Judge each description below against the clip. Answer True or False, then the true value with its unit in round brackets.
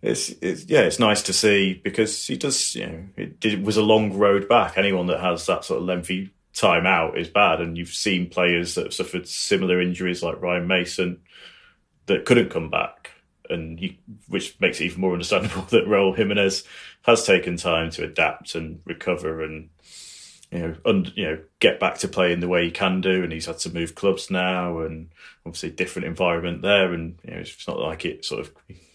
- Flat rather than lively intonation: True (2.3 semitones)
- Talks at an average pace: False (210 wpm)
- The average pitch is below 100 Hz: True (90 Hz)